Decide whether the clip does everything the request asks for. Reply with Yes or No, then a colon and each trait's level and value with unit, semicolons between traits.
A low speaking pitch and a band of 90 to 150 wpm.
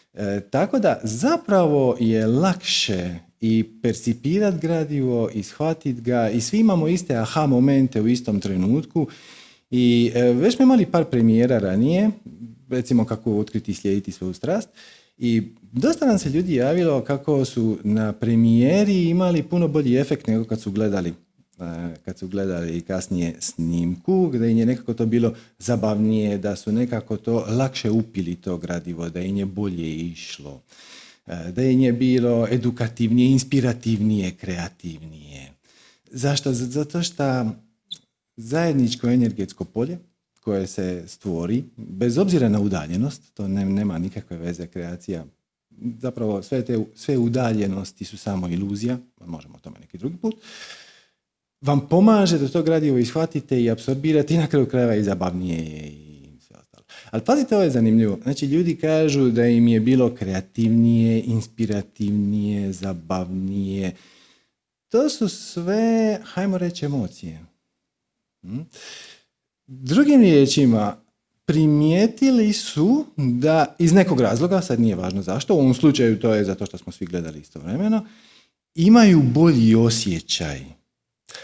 Yes: low, 115 Hz; average, 135 wpm